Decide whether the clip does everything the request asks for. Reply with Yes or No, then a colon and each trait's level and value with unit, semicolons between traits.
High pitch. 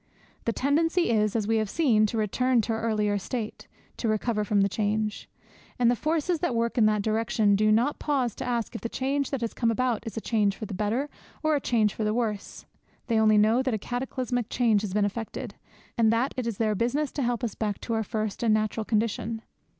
Yes: high, 225 Hz